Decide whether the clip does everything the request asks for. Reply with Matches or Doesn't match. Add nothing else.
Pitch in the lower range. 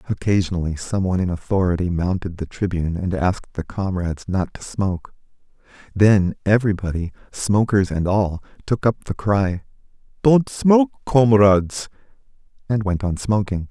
Matches